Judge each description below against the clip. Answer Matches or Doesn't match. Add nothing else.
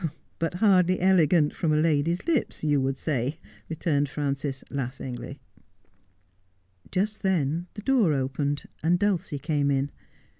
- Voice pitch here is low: Doesn't match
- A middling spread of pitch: Matches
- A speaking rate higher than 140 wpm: Doesn't match